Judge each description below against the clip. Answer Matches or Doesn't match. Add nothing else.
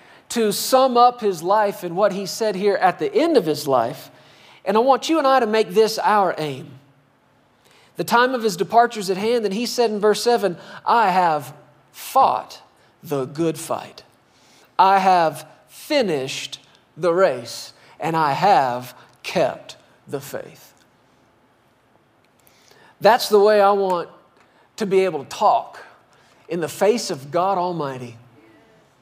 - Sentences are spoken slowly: Doesn't match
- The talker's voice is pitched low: Doesn't match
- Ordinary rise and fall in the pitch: Doesn't match